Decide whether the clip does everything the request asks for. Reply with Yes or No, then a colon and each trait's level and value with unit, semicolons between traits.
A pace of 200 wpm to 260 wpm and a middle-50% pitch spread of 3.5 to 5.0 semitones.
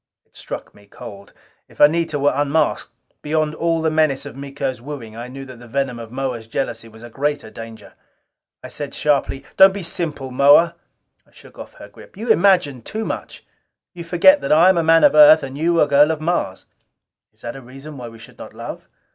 Yes: fast, 205 wpm; average, 4.7 semitones